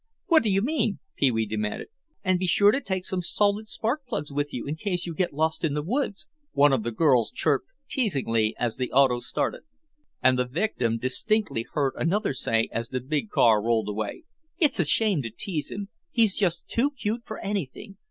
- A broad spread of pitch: Yes, wide, 8.8 semitones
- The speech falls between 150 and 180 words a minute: No, average, 200 wpm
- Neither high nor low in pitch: Yes, medium, 160 Hz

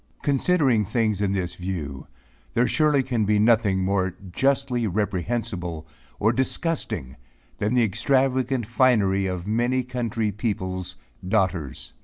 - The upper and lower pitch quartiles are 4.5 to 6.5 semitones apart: Yes, average, 5.0 semitones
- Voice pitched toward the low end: Yes, low, 110 Hz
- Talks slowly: Yes, slow, 120 wpm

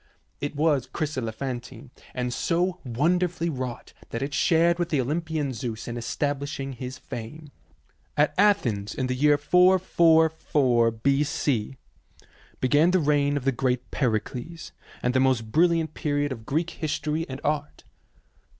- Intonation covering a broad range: No, average, 4.2 semitones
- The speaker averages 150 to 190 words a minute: No, slow, 135 wpm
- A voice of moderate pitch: Yes, medium, 145 Hz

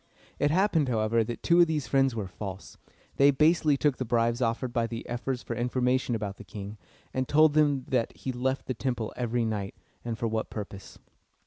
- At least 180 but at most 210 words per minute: Yes, average, 200 wpm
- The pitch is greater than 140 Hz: No, low, 120 Hz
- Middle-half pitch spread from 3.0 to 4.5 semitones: Yes, average, 3.4 semitones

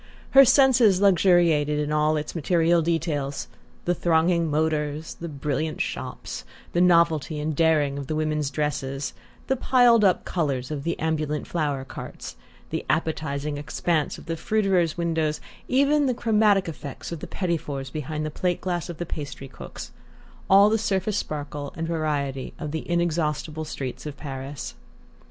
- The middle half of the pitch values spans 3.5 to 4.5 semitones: No, average, 2.9 semitones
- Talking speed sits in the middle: Yes, average, 155 wpm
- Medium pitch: Yes, medium, 160 Hz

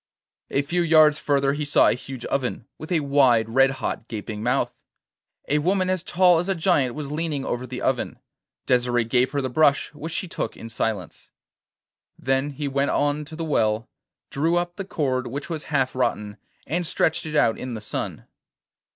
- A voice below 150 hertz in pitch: Yes, medium, 140 Hz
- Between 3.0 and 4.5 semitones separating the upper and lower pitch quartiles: Yes, average, 4.0 semitones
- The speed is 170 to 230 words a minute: Yes, average, 190 wpm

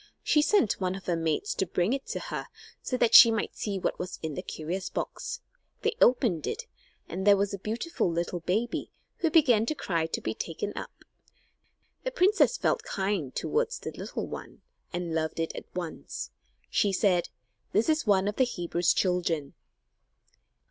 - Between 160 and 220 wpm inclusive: Yes, average, 180 wpm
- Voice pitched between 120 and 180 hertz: No, high, 195 Hz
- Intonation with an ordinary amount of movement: No, wide, 5.7 semitones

